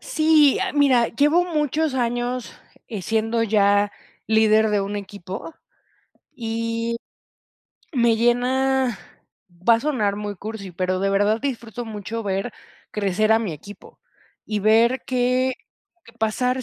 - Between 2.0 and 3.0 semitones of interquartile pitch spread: No, average, 3.5 semitones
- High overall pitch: Yes, high, 225 Hz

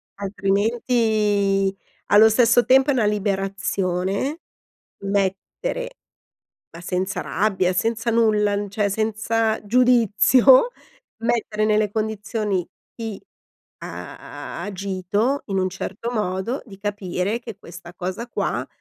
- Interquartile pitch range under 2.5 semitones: No, average, 2.8 semitones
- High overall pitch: Yes, high, 210 Hz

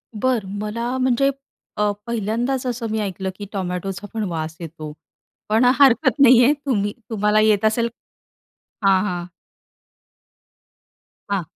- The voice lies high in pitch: Yes, high, 215 Hz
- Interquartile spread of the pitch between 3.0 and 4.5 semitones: Yes, average, 3.9 semitones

